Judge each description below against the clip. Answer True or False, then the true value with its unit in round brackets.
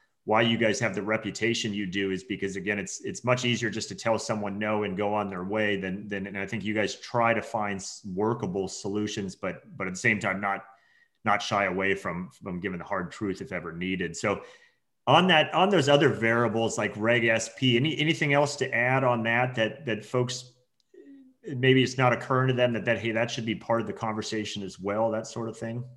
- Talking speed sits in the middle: False (225 wpm)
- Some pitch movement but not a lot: True (3.3 semitones)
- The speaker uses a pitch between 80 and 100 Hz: False (110 Hz)